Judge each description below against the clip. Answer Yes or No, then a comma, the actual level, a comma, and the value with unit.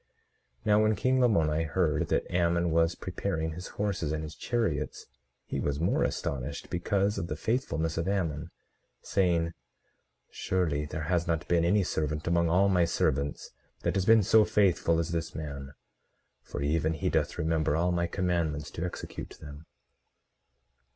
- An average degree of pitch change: Yes, average, 3.1 semitones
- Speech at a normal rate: Yes, average, 160 wpm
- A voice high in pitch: No, very low, 85 Hz